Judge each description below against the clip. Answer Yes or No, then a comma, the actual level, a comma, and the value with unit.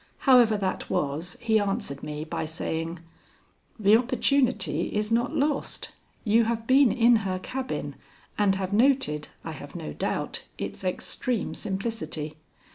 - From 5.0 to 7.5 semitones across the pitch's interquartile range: Yes, wide, 5.4 semitones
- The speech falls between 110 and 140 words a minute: Yes, slow, 135 wpm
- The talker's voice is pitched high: Yes, high, 210 Hz